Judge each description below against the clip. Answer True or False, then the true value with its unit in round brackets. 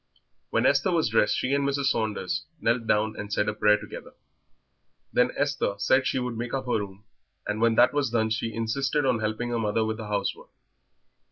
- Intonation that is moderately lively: True (3.5 semitones)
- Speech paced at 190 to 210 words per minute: True (200 wpm)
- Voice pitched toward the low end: True (115 Hz)